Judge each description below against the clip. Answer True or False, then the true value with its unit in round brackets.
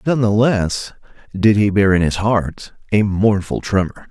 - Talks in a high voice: False (105 Hz)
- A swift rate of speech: False (175 wpm)